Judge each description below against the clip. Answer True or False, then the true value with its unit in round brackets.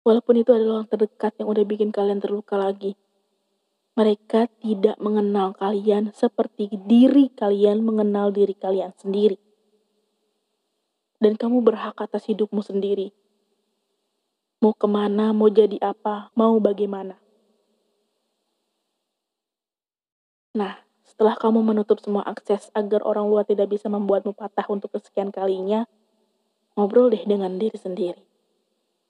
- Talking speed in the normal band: True (115 wpm)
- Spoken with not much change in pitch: True (1.2 semitones)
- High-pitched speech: True (210 Hz)